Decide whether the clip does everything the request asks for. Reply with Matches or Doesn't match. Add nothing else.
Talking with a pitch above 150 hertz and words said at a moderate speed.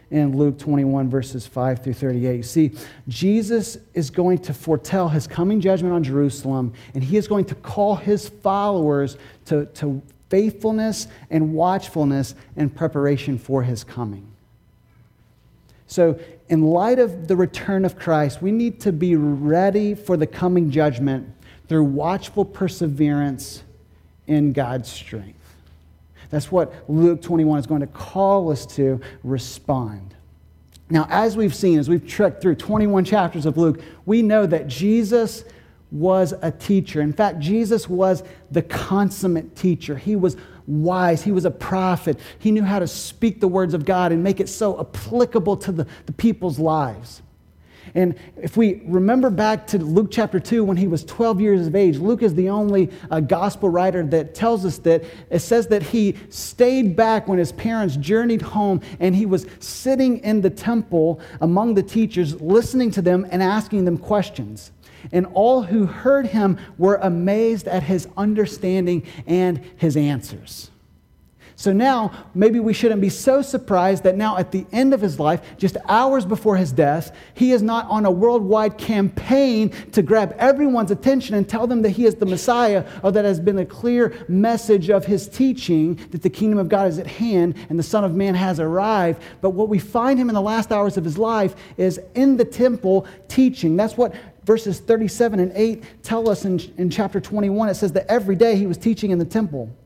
Matches